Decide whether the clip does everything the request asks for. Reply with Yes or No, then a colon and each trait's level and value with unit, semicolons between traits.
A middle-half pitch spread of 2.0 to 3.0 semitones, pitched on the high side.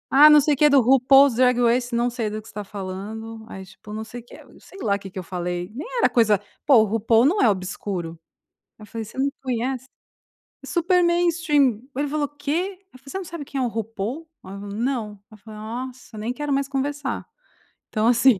No: average, 4.8 semitones; high, 240 Hz